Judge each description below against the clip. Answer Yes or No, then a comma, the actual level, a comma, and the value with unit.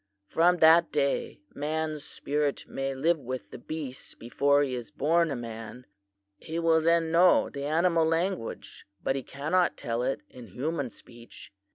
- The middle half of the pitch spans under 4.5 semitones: Yes, average, 4.1 semitones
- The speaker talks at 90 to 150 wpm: No, average, 160 wpm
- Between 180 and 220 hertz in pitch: No, medium, 145 Hz